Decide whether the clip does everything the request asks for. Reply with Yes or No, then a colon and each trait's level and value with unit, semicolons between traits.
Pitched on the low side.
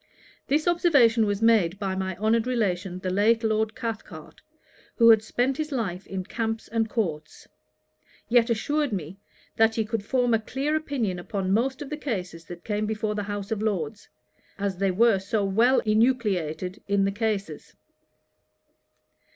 No: high, 215 Hz